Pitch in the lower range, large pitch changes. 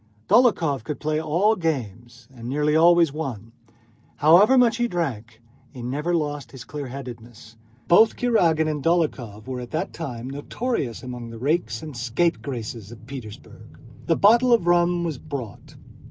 No: medium, 150 Hz; wide, 6.0 semitones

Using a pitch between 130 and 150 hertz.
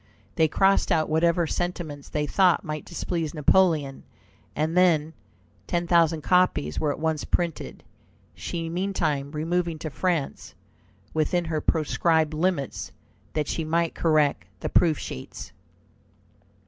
No: medium, 160 Hz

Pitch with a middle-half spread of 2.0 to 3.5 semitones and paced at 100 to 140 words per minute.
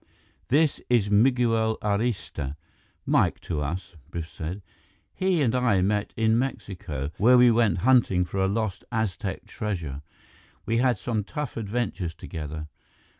No: average, 5.1 semitones; slow, 135 wpm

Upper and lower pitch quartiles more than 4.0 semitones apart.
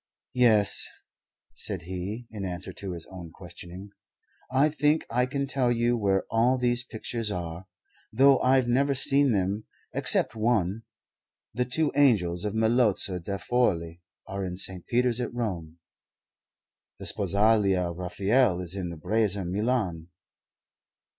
Yes: average, 5.1 semitones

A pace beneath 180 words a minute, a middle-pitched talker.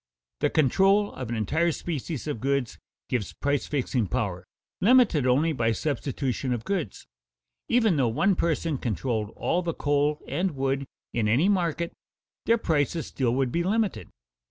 Yes: average, 155 wpm; medium, 145 Hz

